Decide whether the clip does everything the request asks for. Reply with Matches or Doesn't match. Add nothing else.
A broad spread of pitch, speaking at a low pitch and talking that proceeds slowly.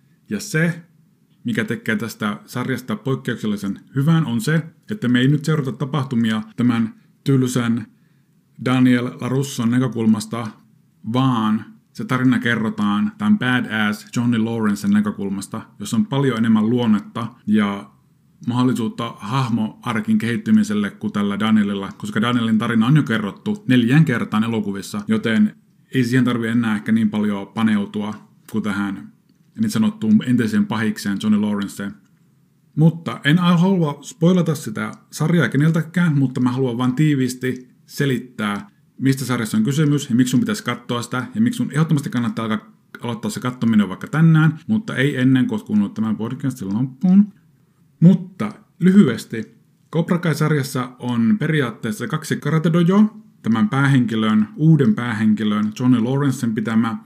Doesn't match